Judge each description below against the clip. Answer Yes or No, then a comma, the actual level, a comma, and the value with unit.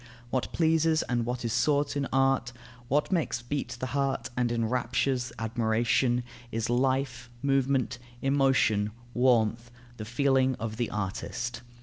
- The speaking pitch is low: Yes, low, 125 Hz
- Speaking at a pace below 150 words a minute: Yes, slow, 135 wpm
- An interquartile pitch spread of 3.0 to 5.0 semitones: No, narrow, 2.6 semitones